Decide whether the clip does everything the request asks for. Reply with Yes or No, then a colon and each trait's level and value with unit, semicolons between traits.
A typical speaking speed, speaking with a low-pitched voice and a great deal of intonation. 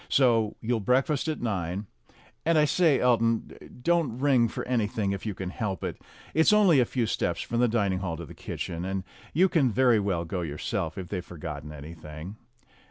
Yes: average, 190 wpm; low, 110 Hz; wide, 6.3 semitones